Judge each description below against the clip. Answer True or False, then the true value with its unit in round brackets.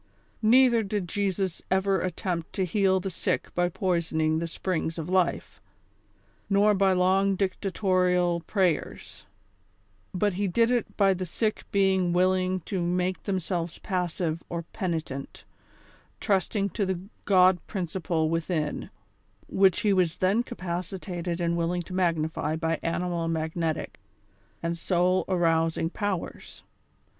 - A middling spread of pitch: False (2.3 semitones)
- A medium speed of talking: False (130 wpm)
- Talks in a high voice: False (180 Hz)